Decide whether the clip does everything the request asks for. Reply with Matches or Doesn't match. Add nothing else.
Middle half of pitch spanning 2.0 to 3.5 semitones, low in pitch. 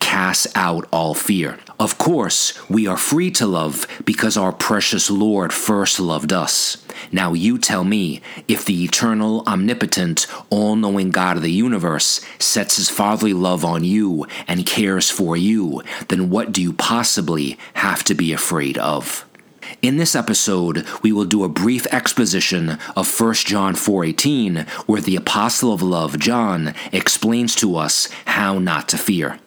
Matches